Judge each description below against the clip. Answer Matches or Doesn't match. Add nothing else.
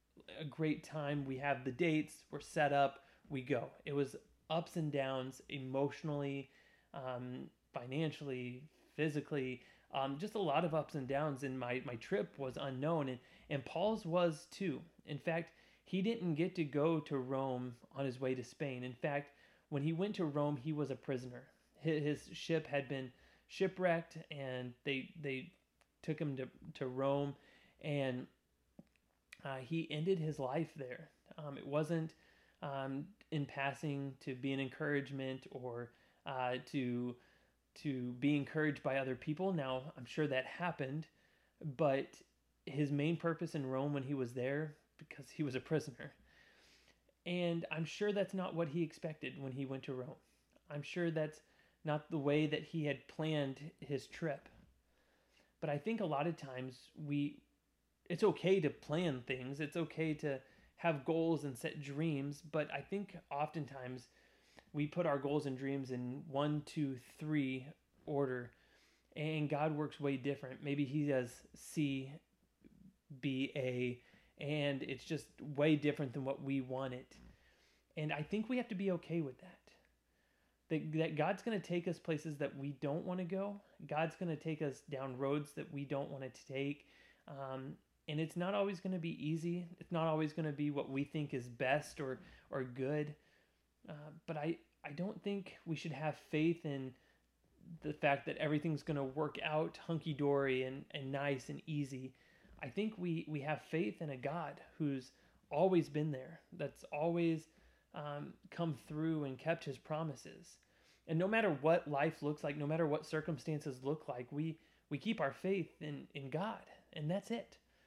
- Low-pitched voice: Doesn't match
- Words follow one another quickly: Doesn't match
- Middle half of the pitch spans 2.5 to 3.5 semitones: Matches